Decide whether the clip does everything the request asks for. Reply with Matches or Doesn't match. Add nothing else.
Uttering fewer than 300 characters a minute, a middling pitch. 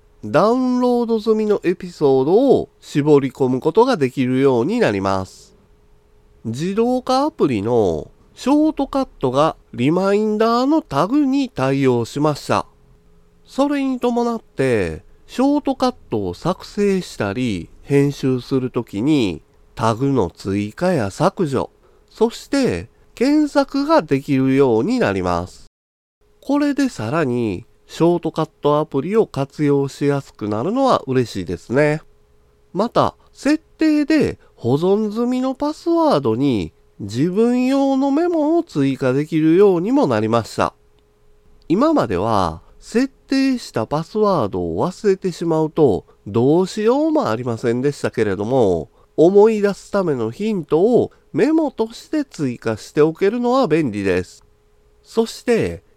Matches